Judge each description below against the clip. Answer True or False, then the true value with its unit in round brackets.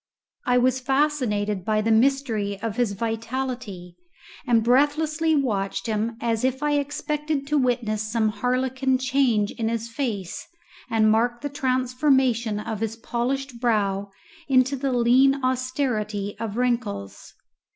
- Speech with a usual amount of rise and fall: True (3.6 semitones)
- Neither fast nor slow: False (130 wpm)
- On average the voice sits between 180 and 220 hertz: False (245 Hz)